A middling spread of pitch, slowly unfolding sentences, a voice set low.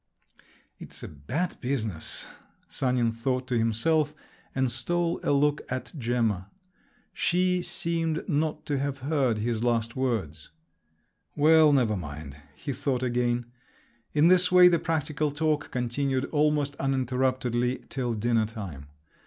Yes: average, 4.4 semitones; slow, 130 wpm; low, 130 Hz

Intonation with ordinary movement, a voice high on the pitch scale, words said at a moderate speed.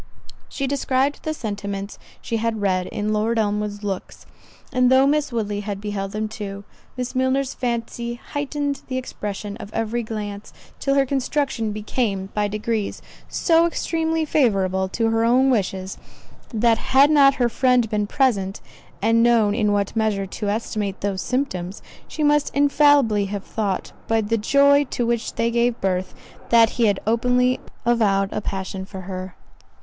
Yes: average, 4.1 semitones; high, 225 Hz; average, 160 wpm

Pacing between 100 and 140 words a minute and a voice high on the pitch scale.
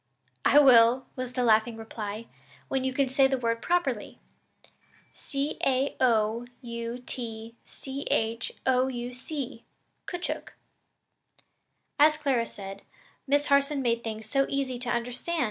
Yes: slow, 135 wpm; very high, 250 Hz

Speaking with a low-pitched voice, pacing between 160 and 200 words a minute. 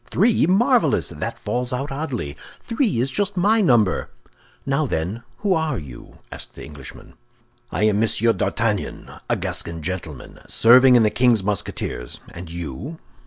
No: low, 120 Hz; average, 150 wpm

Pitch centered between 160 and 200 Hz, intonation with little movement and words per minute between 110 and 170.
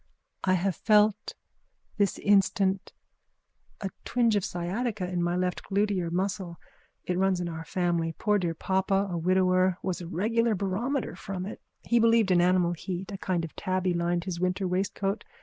Yes: medium, 185 Hz; narrow, 2.3 semitones; average, 165 wpm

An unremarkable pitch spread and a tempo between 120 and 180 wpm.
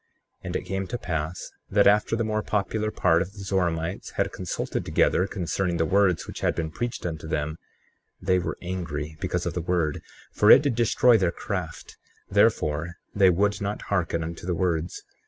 No: average, 3.5 semitones; average, 190 wpm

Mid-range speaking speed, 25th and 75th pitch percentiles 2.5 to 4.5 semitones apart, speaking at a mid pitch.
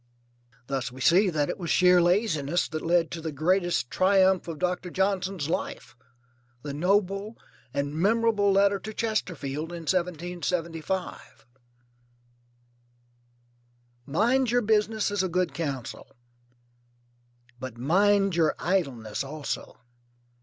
No: slow, 115 wpm; average, 4.2 semitones; medium, 180 Hz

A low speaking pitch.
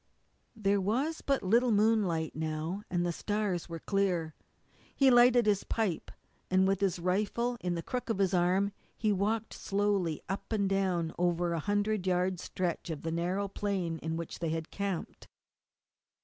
No: high, 190 Hz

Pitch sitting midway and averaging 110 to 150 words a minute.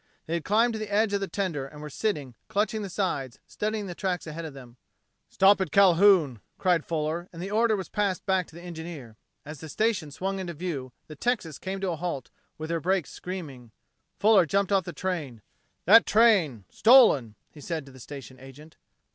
No: medium, 175 Hz; average, 195 wpm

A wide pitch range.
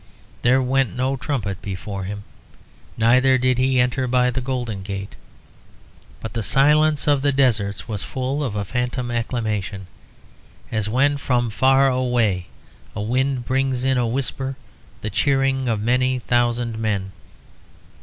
No: average, 3.3 semitones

